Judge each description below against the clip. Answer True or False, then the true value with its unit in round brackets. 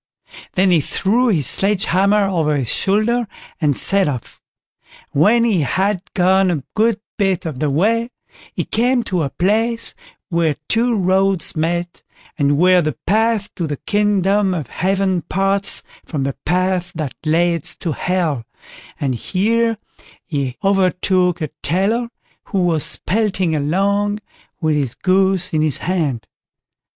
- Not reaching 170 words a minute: True (145 wpm)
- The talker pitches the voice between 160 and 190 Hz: True (185 Hz)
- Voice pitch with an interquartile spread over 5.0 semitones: False (4.3 semitones)